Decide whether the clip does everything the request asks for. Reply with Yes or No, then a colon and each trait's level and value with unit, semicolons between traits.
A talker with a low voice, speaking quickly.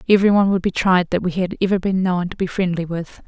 No: medium, 185 Hz; fast, 275 wpm